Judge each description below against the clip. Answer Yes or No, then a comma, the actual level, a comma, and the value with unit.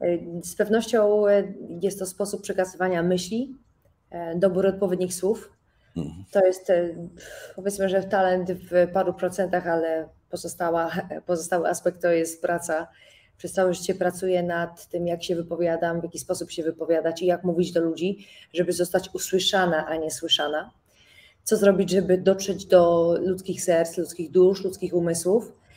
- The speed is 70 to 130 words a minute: No, average, 140 wpm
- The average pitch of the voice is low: No, medium, 180 Hz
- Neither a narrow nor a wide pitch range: No, narrow, 2.1 semitones